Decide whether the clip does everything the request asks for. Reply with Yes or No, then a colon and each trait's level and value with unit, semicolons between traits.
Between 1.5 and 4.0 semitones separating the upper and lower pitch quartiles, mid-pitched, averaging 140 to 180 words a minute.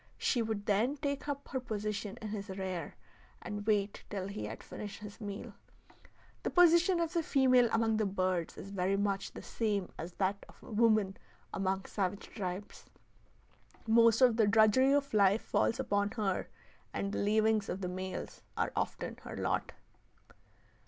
No: average, 2.7 semitones; high, 210 Hz; average, 165 wpm